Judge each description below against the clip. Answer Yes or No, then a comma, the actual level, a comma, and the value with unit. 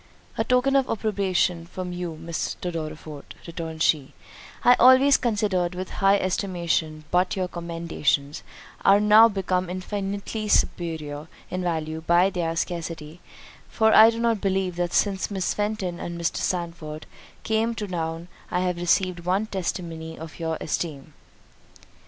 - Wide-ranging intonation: No, average, 3.4 semitones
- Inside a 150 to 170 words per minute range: No, average, 140 wpm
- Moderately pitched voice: Yes, medium, 180 Hz